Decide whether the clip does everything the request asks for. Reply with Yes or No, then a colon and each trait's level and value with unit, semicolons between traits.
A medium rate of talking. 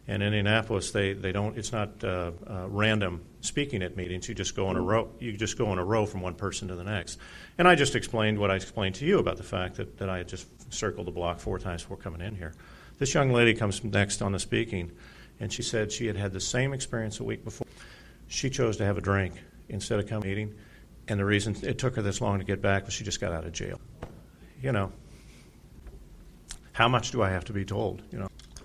No: fast, 245 wpm